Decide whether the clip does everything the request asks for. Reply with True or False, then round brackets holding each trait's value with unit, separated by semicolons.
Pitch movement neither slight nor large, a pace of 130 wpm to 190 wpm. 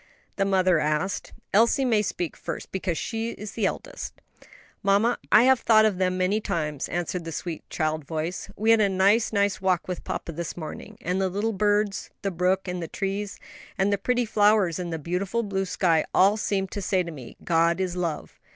False (3.2 semitones; 200 wpm)